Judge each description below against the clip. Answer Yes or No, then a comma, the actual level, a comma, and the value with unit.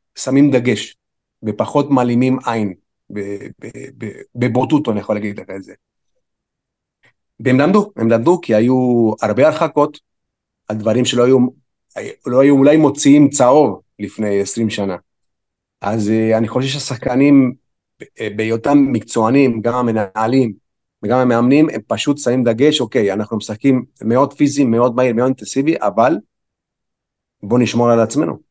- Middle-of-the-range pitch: No, low, 125 Hz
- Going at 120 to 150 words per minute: Yes, average, 130 wpm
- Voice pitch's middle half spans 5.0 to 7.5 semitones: No, average, 3.7 semitones